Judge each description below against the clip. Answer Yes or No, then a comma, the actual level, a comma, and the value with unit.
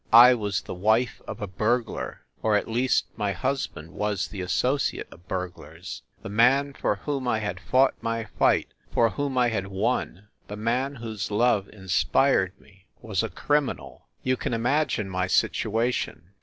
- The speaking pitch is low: Yes, low, 110 Hz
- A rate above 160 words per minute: Yes, average, 170 wpm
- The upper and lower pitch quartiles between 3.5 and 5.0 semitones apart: Yes, average, 4.4 semitones